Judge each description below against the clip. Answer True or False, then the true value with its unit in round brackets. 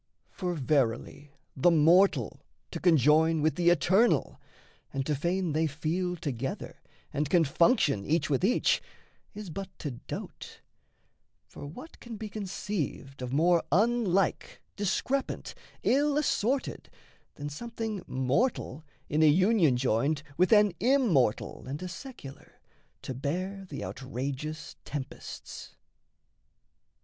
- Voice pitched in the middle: True (165 Hz)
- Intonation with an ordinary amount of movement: False (5.9 semitones)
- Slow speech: True (120 wpm)